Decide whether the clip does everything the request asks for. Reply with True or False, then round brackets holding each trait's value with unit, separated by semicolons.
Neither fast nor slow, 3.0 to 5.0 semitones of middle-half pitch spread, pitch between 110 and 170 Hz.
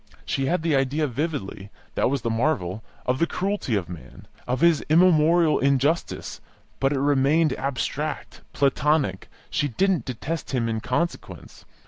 True (145 wpm; 4.3 semitones; 140 Hz)